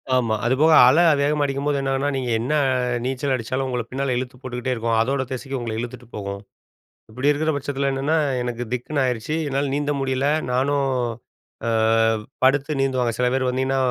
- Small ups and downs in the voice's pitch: Yes, narrow, 2.1 semitones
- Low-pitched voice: Yes, low, 130 Hz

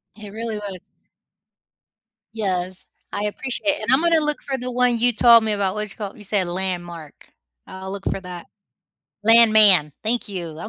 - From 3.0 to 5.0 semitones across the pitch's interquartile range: Yes, average, 3.8 semitones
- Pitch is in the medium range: No, high, 210 Hz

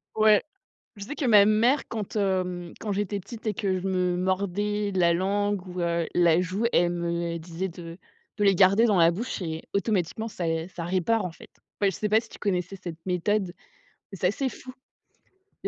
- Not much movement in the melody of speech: No, average, 3.0 semitones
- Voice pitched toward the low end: No, high, 190 Hz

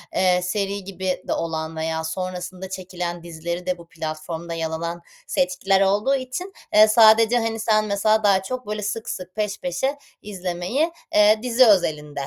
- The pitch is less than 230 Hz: Yes, high, 190 Hz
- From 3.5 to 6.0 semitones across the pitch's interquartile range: Yes, average, 3.9 semitones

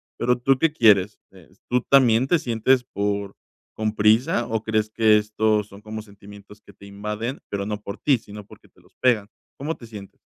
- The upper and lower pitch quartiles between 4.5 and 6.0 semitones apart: No, average, 2.7 semitones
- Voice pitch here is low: Yes, low, 110 Hz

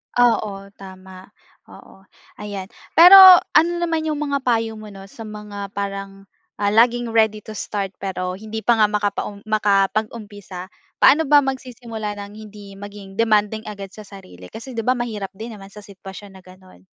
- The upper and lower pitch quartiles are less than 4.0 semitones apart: Yes, narrow, 2.6 semitones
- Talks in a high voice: Yes, high, 210 Hz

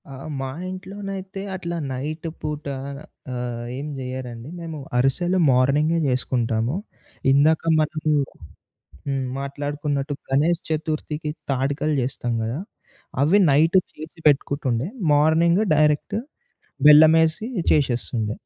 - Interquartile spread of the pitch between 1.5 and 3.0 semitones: No, average, 3.4 semitones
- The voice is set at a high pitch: No, medium, 150 Hz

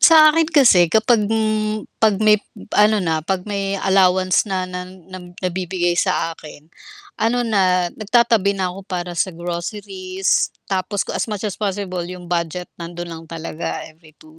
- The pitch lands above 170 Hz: Yes, medium, 185 Hz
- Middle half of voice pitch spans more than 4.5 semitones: No, average, 3.3 semitones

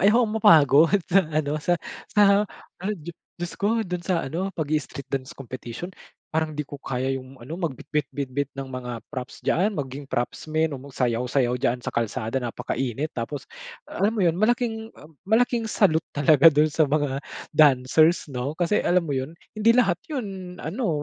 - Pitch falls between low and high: Yes, medium, 155 Hz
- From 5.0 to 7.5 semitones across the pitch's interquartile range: Yes, wide, 5.5 semitones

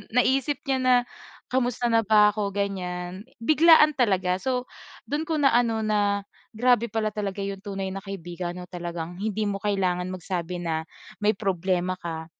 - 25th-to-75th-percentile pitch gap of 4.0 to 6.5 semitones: Yes, average, 4.3 semitones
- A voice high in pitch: Yes, high, 200 Hz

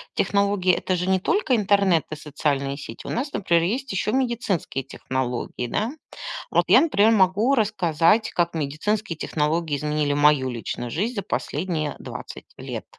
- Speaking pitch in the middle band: Yes, medium, 175 Hz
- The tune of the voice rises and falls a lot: Yes, wide, 6.0 semitones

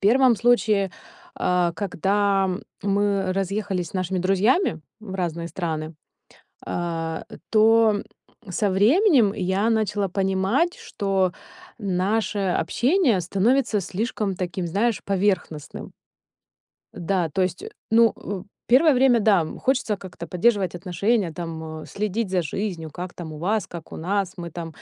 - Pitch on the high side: Yes, high, 195 Hz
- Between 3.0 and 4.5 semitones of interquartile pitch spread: Yes, average, 3.5 semitones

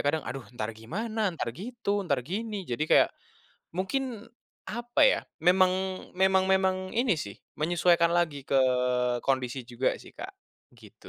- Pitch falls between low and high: Yes, medium, 175 Hz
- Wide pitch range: Yes, wide, 6.7 semitones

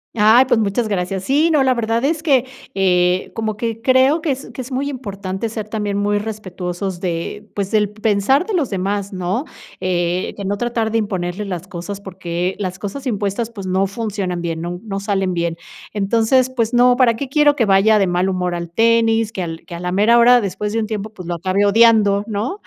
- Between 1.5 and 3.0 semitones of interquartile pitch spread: No, average, 3.7 semitones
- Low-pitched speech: No, high, 205 Hz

